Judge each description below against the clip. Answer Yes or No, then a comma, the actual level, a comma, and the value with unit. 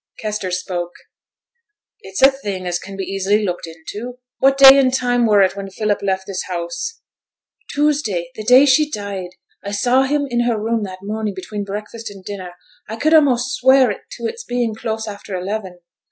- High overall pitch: Yes, high, 210 Hz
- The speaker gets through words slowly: No, average, 180 wpm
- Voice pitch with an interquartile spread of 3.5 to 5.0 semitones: Yes, average, 4.6 semitones